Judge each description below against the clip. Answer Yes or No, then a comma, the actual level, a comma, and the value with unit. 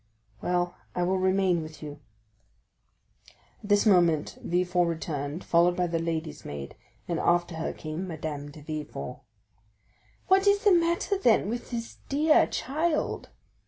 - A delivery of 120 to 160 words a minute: Yes, average, 140 wpm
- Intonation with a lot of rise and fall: Yes, wide, 5.9 semitones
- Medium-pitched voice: Yes, medium, 175 Hz